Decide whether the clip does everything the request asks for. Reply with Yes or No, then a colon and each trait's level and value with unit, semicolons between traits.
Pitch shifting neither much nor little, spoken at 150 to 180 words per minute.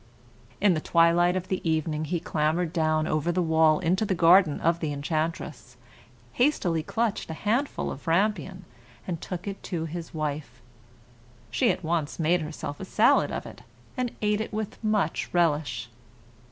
Yes: average, 3.1 semitones; average, 160 wpm